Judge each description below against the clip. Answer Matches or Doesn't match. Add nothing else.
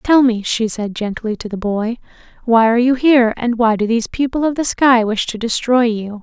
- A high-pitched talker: Matches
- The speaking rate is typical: Doesn't match